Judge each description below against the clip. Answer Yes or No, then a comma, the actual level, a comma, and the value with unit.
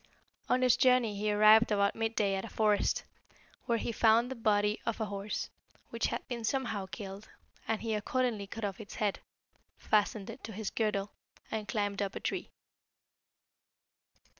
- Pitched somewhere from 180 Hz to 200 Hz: No, high, 215 Hz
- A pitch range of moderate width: No, narrow, 2.1 semitones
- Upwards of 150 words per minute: Yes, average, 170 wpm